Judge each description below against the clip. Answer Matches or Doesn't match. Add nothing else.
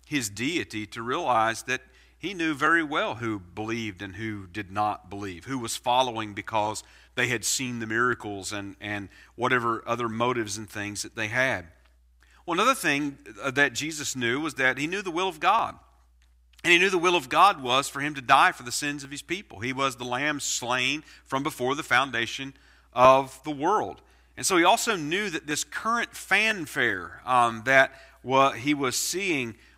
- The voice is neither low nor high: Doesn't match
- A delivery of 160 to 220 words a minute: Matches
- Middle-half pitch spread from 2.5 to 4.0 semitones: Doesn't match